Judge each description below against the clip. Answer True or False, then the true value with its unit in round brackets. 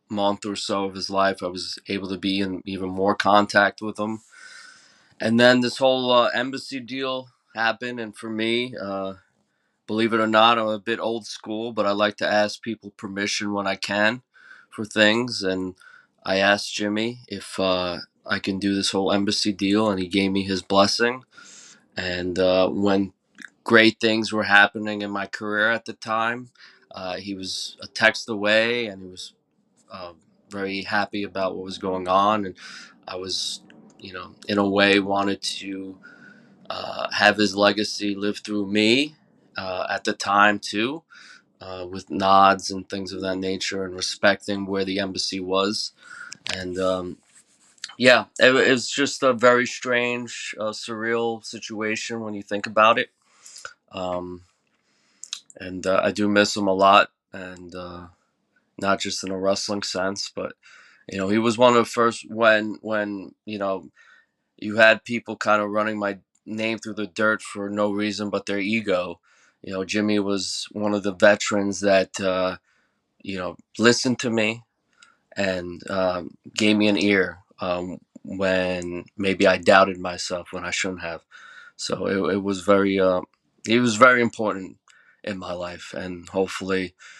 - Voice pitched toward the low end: True (100 Hz)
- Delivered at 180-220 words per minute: False (170 wpm)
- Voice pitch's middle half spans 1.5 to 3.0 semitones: True (2.4 semitones)